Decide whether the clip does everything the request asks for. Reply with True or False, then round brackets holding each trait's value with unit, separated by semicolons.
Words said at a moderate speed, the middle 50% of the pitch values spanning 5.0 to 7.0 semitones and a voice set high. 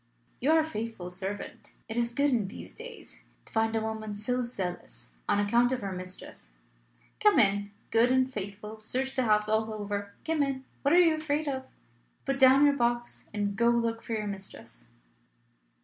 False (190 wpm; 4.4 semitones; 225 Hz)